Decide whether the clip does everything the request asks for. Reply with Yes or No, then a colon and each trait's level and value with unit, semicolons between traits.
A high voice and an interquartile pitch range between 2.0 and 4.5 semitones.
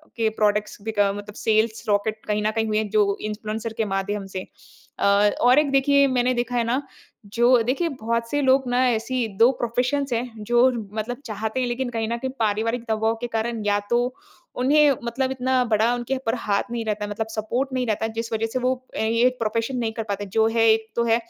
Yes: high, 230 Hz; narrow, 2.5 semitones